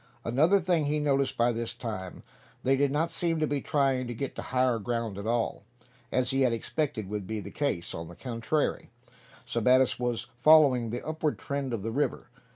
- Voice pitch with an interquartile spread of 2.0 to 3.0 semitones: No, average, 4.0 semitones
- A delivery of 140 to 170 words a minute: No, average, 195 wpm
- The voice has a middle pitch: No, low, 125 Hz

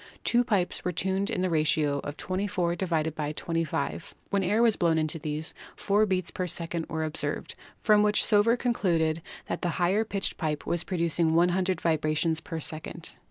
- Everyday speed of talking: Yes, average, 165 wpm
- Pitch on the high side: No, medium, 175 Hz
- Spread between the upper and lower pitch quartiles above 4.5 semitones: No, average, 3.4 semitones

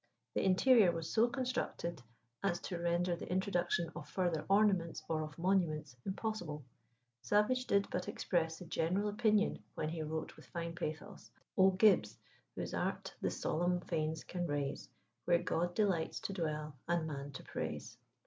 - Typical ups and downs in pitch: Yes, average, 3.5 semitones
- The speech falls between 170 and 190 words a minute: No, average, 160 wpm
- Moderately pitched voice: Yes, medium, 175 Hz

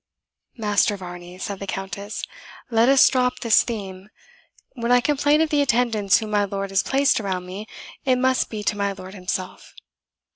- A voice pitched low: No, high, 210 Hz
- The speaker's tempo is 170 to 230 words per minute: Yes, average, 175 wpm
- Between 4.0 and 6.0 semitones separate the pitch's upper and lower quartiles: Yes, average, 4.3 semitones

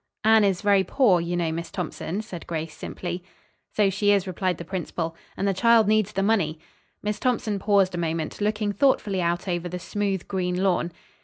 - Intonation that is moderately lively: Yes, average, 3.0 semitones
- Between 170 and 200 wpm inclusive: Yes, average, 190 wpm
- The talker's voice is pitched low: No, high, 190 Hz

